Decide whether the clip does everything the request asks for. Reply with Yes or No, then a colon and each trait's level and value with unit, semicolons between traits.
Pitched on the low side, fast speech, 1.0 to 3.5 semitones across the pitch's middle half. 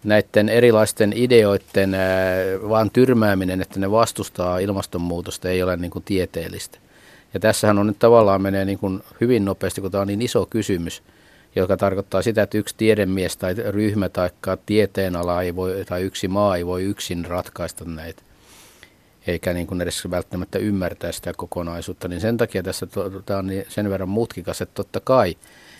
Yes: very low, 95 Hz; fast, 170 wpm; narrow, 2.5 semitones